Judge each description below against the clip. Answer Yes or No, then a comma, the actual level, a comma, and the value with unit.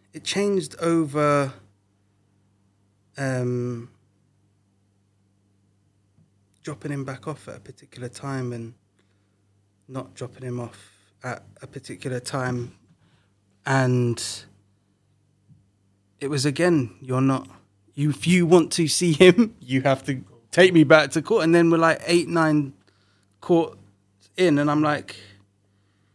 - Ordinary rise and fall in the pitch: No, wide, 6.6 semitones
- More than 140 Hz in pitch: No, low, 125 Hz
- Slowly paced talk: Yes, slow, 120 wpm